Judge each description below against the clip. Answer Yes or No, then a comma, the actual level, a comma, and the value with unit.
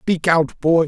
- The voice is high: No, medium, 165 Hz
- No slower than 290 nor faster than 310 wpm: No, fast, 205 wpm